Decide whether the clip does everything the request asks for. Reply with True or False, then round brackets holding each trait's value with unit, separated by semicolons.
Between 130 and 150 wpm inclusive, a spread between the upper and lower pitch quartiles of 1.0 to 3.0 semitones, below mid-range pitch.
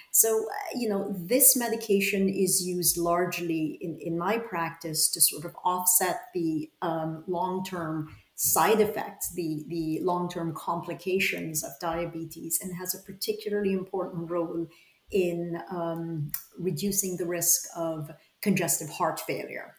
False (135 wpm; 2.7 semitones; 175 Hz)